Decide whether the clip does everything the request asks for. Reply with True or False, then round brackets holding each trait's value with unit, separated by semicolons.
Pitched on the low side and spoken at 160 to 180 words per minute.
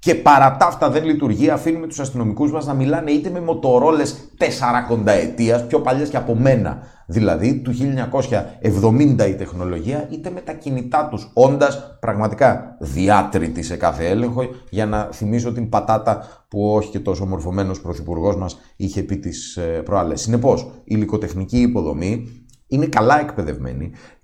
False (115 Hz; 150 wpm)